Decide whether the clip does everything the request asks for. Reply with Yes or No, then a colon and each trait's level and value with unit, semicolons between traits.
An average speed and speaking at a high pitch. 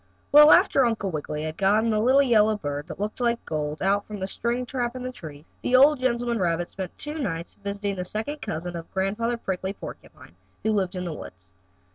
No: fast, 210 wpm; high, 205 Hz